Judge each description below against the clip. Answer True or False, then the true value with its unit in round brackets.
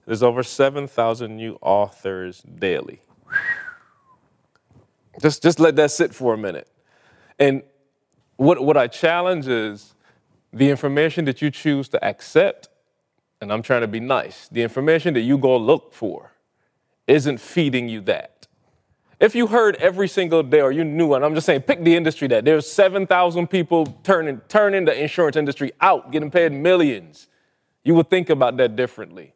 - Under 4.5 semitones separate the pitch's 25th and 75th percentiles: False (4.9 semitones)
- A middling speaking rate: True (160 wpm)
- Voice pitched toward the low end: False (155 Hz)